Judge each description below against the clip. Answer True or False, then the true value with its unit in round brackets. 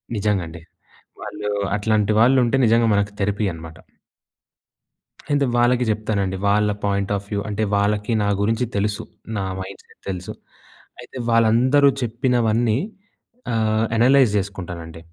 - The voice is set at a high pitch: False (105 Hz)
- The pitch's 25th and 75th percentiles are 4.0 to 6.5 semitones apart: False (2.5 semitones)